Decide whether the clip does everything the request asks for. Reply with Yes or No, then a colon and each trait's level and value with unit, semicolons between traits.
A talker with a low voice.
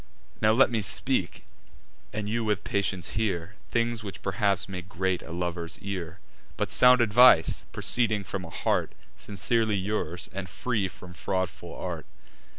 Yes: low, 100 Hz